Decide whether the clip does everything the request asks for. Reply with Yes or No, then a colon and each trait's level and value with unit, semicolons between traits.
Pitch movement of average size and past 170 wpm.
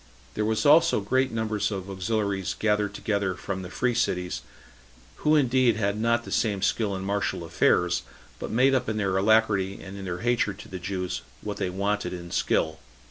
Yes: average, 3.0 semitones; average, 190 wpm